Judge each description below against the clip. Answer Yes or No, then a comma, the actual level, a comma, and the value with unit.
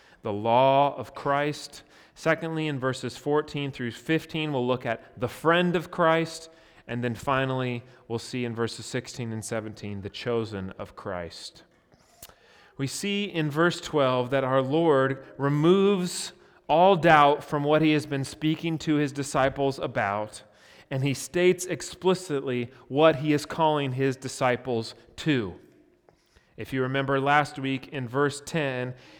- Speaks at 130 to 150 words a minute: Yes, average, 145 wpm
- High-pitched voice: No, low, 135 Hz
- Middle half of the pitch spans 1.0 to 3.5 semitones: No, average, 4.0 semitones